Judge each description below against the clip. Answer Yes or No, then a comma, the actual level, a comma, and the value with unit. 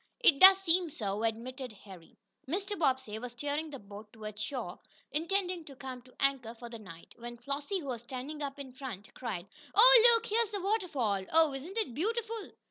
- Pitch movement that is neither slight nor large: No, wide, 7.8 semitones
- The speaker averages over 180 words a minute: Yes, average, 190 wpm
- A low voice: No, very high, 270 Hz